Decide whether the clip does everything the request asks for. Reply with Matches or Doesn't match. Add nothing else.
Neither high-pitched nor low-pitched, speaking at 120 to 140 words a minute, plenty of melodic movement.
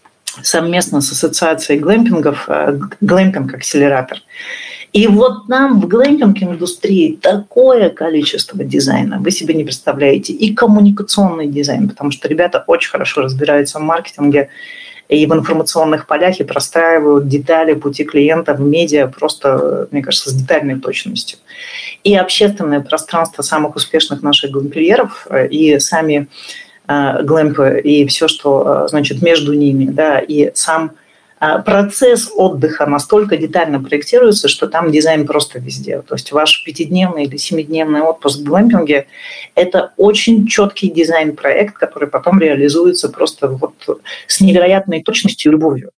Matches